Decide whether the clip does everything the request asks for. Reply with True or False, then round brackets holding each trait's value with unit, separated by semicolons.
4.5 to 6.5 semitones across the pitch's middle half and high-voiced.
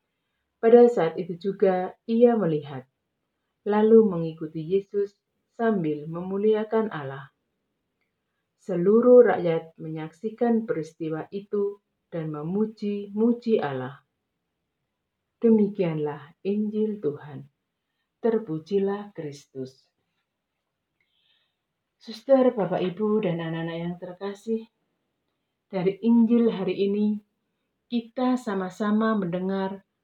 True (5.0 semitones; 195 Hz)